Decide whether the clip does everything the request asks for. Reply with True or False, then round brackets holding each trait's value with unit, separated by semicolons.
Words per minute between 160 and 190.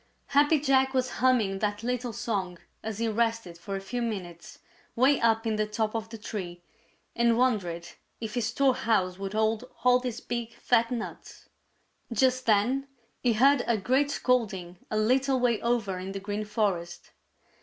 True (165 wpm)